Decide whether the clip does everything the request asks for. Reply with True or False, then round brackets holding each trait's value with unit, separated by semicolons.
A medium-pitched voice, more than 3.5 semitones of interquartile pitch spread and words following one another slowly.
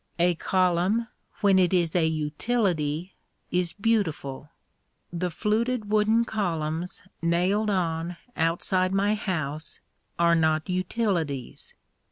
True (180 Hz; 4.1 semitones; 105 wpm)